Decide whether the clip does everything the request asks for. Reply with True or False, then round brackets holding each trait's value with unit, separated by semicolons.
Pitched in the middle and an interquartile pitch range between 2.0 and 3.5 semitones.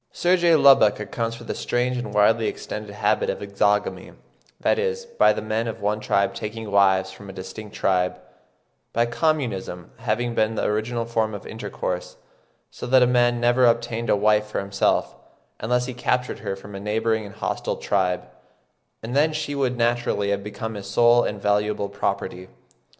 False (110 Hz; 3.0 semitones)